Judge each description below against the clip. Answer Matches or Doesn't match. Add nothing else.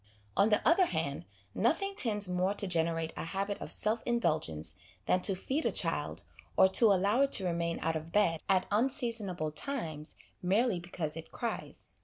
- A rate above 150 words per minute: Matches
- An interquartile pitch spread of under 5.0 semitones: Doesn't match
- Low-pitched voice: Doesn't match